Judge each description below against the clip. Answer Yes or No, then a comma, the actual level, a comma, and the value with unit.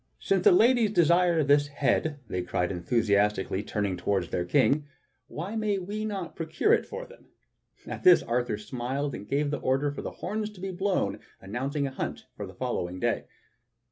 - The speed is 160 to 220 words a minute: Yes, average, 180 wpm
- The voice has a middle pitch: Yes, medium, 145 Hz